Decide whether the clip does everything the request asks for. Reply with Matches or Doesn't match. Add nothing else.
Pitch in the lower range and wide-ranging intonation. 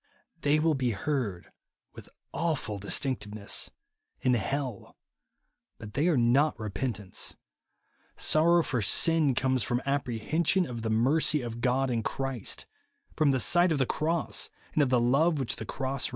Doesn't match